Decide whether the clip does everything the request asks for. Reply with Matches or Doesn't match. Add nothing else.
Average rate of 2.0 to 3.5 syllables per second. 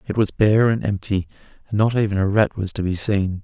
Doesn't match